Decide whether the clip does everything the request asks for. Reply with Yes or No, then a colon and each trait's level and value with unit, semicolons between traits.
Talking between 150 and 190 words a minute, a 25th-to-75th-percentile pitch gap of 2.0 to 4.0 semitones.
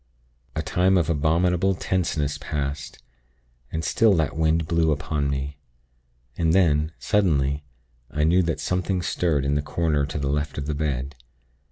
Yes: average, 155 wpm; average, 3.0 semitones